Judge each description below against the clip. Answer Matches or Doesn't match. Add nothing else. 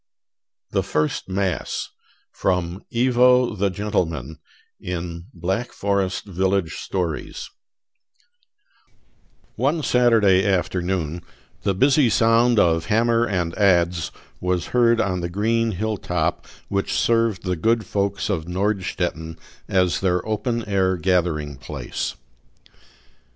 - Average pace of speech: Doesn't match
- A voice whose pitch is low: Matches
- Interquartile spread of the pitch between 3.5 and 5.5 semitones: Matches